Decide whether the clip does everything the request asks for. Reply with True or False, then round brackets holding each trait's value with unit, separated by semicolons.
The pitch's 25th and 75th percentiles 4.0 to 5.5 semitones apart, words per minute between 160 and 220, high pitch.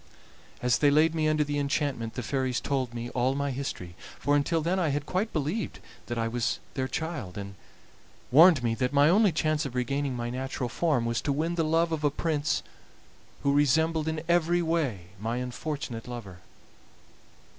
False (4.4 semitones; 185 wpm; 140 Hz)